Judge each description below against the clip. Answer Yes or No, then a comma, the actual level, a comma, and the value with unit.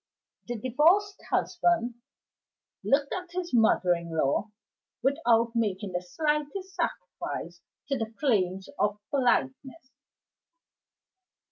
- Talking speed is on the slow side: Yes, slow, 100 wpm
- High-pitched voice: Yes, very high, 250 Hz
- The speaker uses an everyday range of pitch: No, wide, 7.0 semitones